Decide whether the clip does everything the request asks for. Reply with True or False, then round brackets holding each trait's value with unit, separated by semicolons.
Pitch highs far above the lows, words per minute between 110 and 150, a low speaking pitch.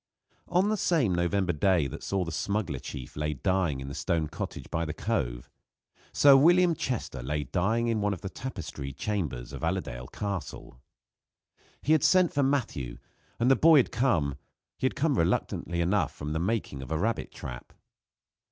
False (8.0 semitones; 175 wpm; 95 Hz)